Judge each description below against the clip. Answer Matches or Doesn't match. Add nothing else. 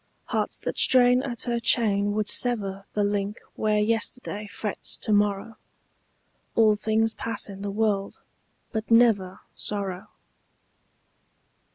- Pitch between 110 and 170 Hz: Doesn't match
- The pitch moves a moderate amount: Doesn't match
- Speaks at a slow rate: Matches